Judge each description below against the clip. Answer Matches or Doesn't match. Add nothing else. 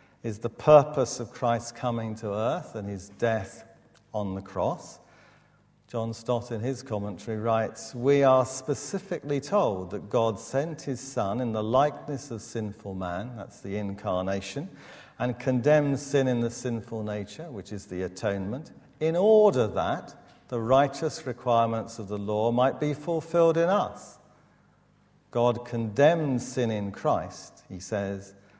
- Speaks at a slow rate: Doesn't match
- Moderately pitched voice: Doesn't match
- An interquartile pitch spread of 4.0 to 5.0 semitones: Matches